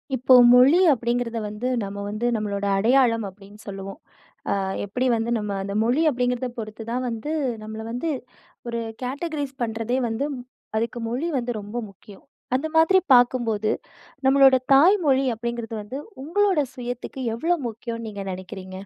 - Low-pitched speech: No, high, 235 Hz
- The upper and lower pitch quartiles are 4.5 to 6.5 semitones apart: No, average, 3.5 semitones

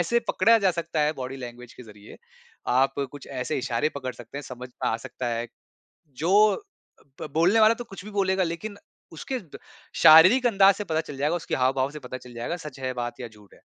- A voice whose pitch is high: No, medium, 150 Hz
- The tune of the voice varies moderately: No, wide, 7.1 semitones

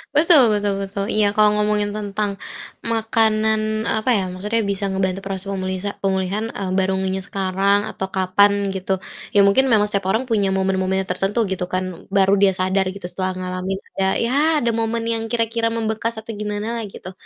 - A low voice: No, high, 200 Hz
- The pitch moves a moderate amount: No, narrow, 2.3 semitones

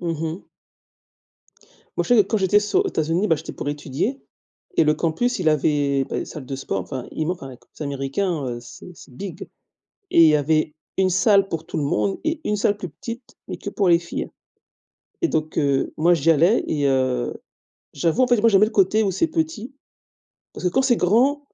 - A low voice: No, medium, 170 Hz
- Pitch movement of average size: No, wide, 6.4 semitones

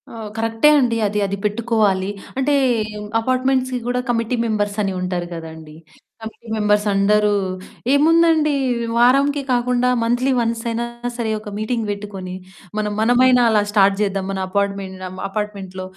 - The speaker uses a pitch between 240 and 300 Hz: No, high, 220 Hz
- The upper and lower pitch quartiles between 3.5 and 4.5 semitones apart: Yes, average, 3.8 semitones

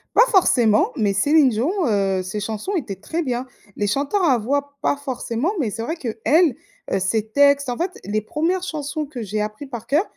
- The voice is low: No, very high, 255 Hz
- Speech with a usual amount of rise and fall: No, wide, 5.9 semitones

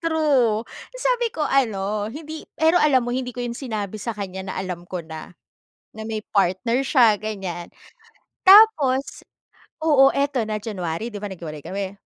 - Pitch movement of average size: No, wide, 6.1 semitones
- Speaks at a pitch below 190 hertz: No, high, 225 Hz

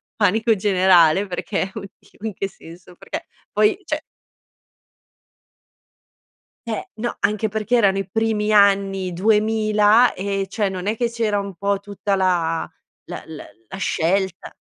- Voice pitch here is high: Yes, high, 200 Hz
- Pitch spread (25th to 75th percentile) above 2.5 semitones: No, narrow, 2.2 semitones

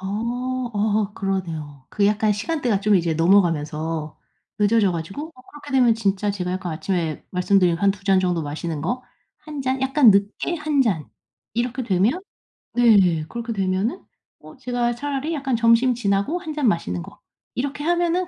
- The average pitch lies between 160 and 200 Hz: No, high, 210 Hz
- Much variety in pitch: Yes, wide, 5.9 semitones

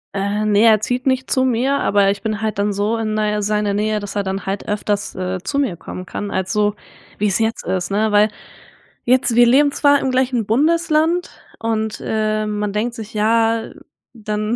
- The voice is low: No, high, 215 Hz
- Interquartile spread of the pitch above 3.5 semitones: No, average, 2.7 semitones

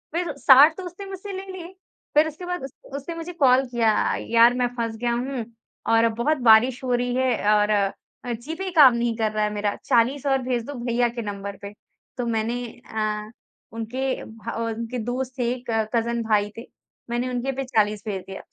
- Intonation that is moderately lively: Yes, average, 3.3 semitones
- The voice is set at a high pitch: Yes, high, 240 Hz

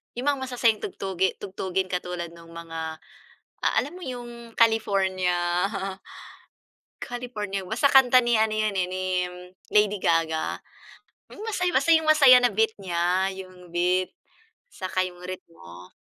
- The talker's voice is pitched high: Yes, high, 195 Hz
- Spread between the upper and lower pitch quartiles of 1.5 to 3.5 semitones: No, average, 5.1 semitones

